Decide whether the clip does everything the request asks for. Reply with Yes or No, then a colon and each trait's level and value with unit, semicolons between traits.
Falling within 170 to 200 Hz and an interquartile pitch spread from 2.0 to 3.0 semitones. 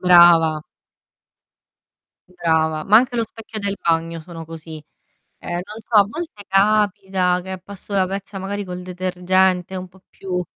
Yes: medium, 185 Hz; narrow, 2.6 semitones